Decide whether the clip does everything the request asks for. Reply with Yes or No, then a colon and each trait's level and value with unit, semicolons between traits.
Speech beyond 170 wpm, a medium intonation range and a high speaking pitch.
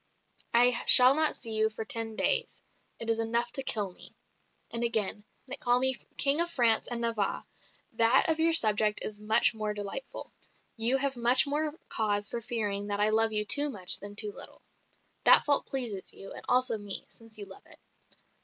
Yes: average, 190 wpm; average, 3.3 semitones; high, 230 Hz